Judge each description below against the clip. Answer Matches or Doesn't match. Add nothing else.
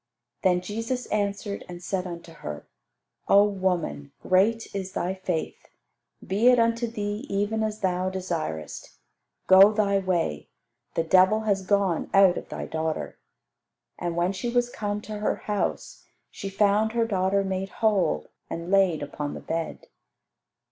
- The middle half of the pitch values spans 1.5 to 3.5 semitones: Matches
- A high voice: Matches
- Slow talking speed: Doesn't match